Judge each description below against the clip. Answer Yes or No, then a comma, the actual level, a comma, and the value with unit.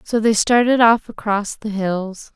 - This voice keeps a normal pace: Yes, average, 180 wpm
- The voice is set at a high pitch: Yes, high, 215 Hz